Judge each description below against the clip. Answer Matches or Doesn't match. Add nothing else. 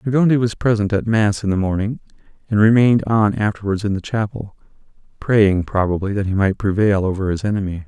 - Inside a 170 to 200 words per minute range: Matches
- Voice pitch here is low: Matches